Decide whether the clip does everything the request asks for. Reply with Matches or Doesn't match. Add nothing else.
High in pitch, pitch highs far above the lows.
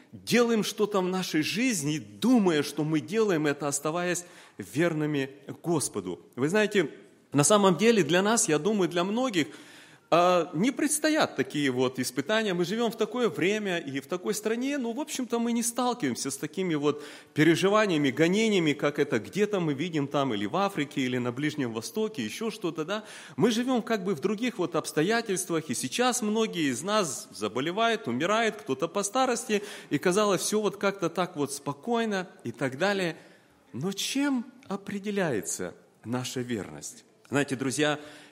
Doesn't match